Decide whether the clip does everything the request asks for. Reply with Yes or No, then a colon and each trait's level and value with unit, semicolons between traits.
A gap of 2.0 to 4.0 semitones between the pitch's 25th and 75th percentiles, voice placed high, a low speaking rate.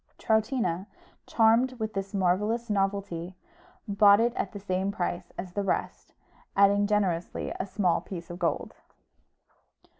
Yes: average, 2.8 semitones; high, 200 Hz; slow, 130 wpm